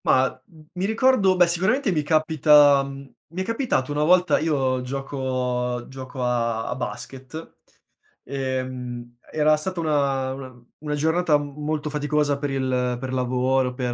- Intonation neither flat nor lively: Yes, average, 3.4 semitones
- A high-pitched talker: No, medium, 140 Hz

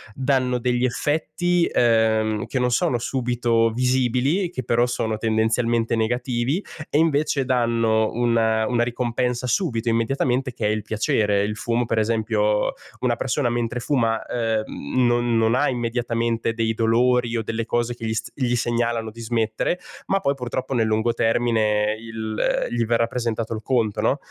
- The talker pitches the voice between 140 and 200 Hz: No, low, 120 Hz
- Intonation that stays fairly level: Yes, narrow, 1.8 semitones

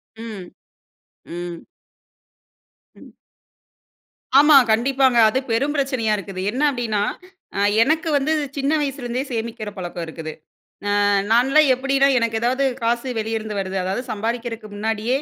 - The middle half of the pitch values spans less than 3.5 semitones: No, average, 4.1 semitones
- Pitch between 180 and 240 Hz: Yes, high, 230 Hz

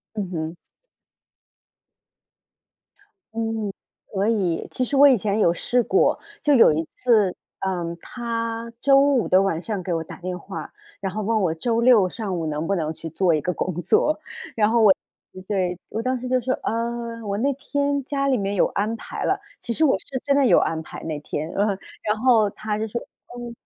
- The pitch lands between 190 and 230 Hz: Yes, high, 215 Hz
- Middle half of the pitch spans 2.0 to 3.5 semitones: No, average, 4.8 semitones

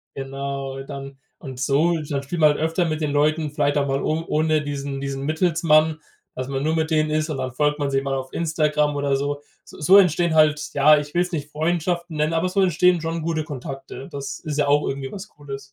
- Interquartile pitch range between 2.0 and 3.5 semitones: Yes, narrow, 2.5 semitones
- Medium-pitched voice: Yes, medium, 150 Hz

